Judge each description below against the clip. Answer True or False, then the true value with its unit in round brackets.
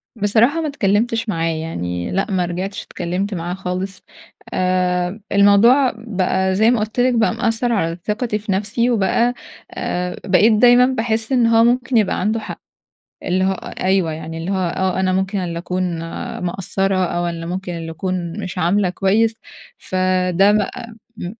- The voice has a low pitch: False (190 Hz)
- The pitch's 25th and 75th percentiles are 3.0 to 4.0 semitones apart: True (3.7 semitones)